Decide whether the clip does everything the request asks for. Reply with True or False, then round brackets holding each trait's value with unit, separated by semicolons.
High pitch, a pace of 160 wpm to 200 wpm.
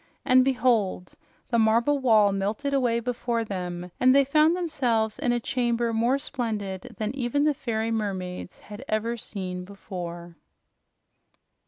False (230 Hz; 140 wpm)